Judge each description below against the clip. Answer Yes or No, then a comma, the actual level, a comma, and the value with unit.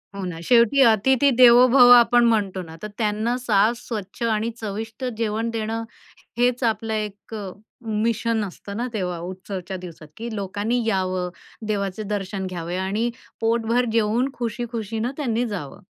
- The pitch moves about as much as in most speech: Yes, average, 3.1 semitones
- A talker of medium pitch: No, high, 220 Hz